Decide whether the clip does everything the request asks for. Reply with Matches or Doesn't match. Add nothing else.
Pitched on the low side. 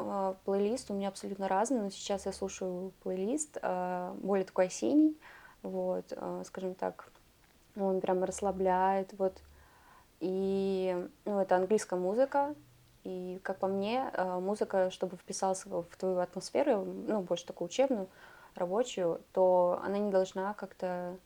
Doesn't match